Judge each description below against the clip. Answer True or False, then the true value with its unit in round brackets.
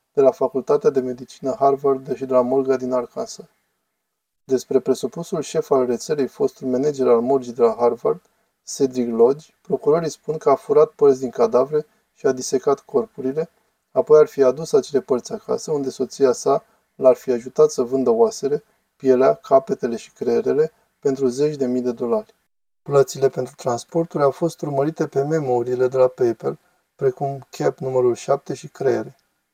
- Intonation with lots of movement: True (8.9 semitones)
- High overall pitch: False (150 Hz)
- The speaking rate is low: False (165 wpm)